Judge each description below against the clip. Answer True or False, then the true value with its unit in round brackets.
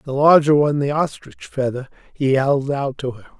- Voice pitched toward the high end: False (140 Hz)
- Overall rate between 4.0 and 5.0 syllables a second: False (5.2 syllables/s)